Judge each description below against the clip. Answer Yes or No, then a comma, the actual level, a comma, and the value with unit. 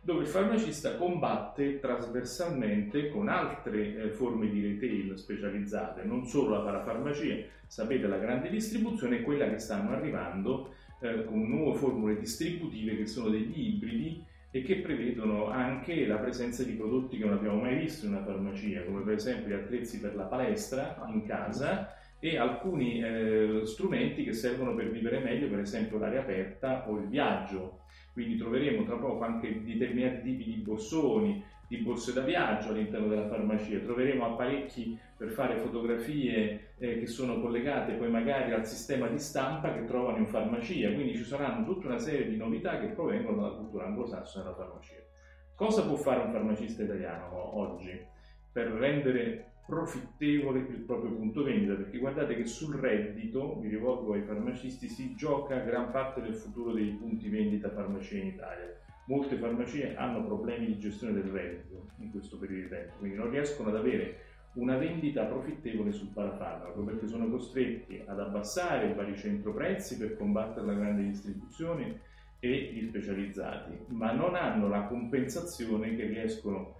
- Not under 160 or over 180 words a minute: Yes, average, 165 wpm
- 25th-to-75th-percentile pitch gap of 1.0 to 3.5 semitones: No, average, 4.4 semitones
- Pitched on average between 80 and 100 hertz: No, low, 115 Hz